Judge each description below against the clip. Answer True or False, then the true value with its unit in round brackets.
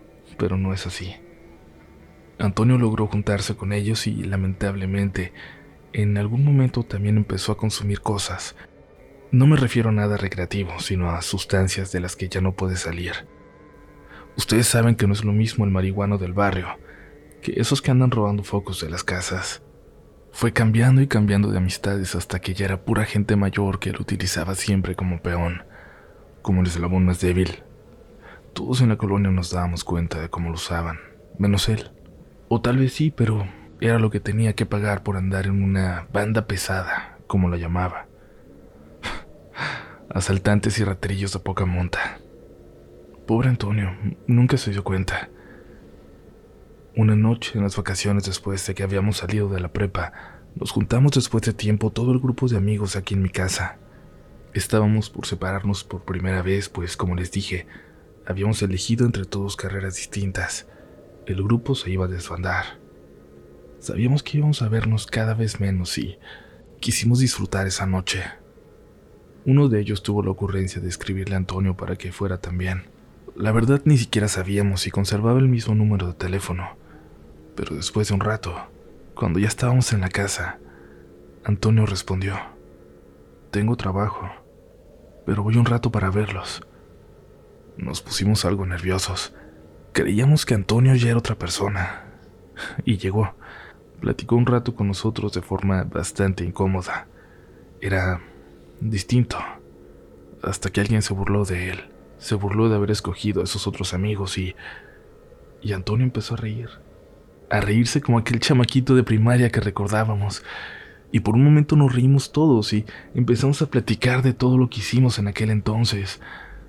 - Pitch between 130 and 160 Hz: False (100 Hz)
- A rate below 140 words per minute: False (160 wpm)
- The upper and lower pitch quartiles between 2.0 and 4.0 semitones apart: True (3.0 semitones)